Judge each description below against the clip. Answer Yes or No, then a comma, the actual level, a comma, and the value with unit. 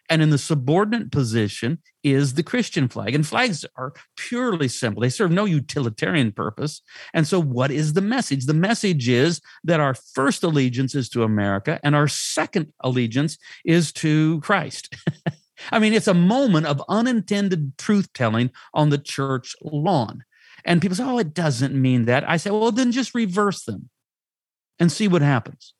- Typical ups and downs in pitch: No, wide, 6.2 semitones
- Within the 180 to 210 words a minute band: No, average, 170 wpm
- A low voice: No, medium, 155 Hz